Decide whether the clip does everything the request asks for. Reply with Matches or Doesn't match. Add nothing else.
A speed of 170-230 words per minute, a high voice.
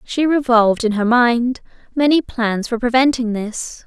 Doesn't match